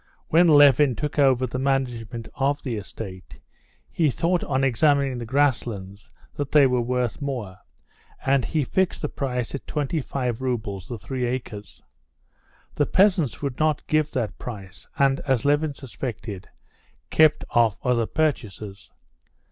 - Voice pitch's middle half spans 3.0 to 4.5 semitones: Yes, average, 3.8 semitones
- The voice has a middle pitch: No, low, 130 Hz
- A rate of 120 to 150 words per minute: Yes, average, 145 wpm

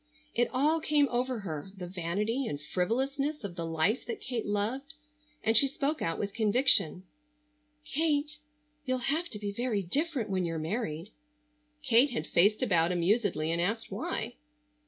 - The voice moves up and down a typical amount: No, wide, 7.2 semitones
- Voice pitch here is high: Yes, high, 220 Hz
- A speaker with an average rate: Yes, average, 155 wpm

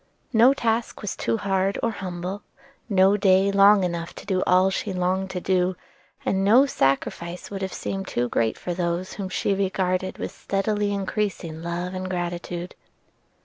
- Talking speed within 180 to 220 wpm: No, average, 165 wpm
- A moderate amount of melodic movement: No, narrow, 1.9 semitones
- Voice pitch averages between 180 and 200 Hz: Yes, high, 190 Hz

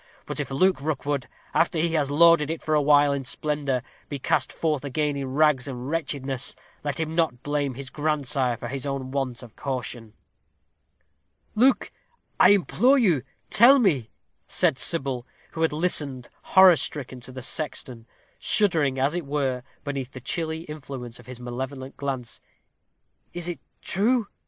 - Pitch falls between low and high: Yes, medium, 145 Hz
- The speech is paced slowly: No, average, 155 wpm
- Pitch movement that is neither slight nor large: Yes, average, 3.6 semitones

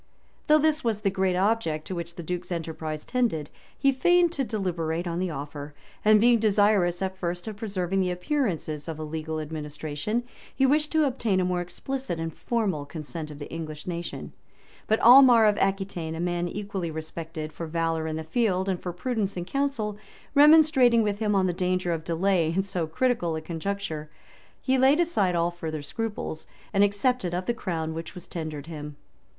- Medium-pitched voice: Yes, medium, 180 Hz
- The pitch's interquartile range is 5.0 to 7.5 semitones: Yes, average, 5.3 semitones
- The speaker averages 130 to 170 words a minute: No, average, 190 wpm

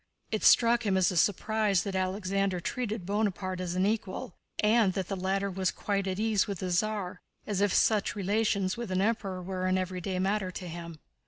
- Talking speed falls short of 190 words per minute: No, average, 195 wpm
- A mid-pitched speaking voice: No, high, 195 Hz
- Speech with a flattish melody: Yes, narrow, 2.1 semitones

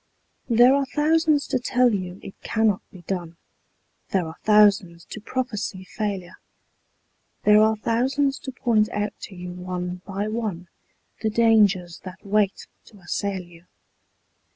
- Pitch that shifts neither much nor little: Yes, average, 4.1 semitones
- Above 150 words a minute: No, average, 140 wpm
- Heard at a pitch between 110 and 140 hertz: No, high, 210 Hz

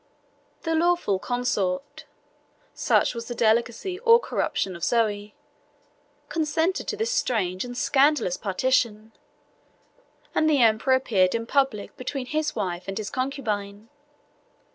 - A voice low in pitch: No, high, 245 Hz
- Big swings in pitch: Yes, wide, 6.3 semitones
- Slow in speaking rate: Yes, slow, 120 wpm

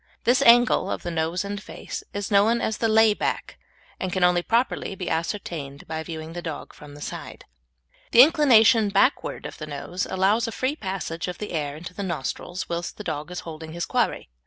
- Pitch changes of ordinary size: Yes, average, 5.0 semitones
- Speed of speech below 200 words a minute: No, fast, 205 wpm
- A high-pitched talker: No, medium, 180 Hz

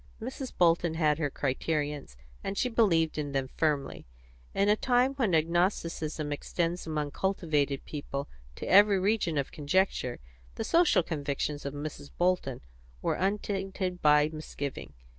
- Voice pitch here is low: No, medium, 160 Hz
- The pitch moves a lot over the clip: No, average, 4.7 semitones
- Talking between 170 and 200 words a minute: No, average, 140 wpm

